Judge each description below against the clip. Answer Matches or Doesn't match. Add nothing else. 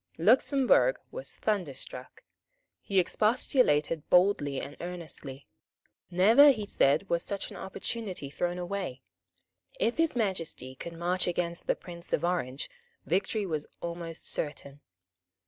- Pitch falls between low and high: Matches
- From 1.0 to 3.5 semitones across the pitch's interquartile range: Doesn't match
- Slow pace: Matches